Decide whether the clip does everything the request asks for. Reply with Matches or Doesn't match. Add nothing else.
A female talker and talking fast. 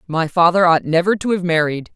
Matches